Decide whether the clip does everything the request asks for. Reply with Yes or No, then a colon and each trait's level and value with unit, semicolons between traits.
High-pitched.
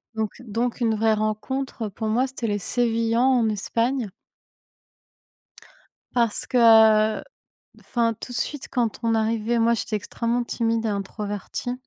Yes: high, 230 Hz